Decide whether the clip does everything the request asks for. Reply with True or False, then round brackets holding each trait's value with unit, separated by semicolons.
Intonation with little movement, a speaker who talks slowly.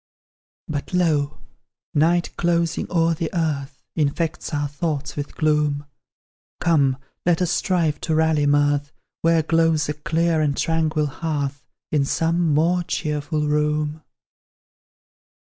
True (2.1 semitones; 120 wpm)